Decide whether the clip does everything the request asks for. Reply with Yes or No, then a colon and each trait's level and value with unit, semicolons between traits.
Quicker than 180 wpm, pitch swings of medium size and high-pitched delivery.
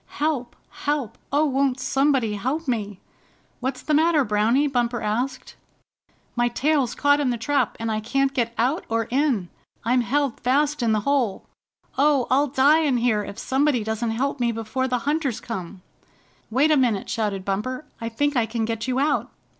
No: average, 175 wpm; average, 3.9 semitones; very high, 250 Hz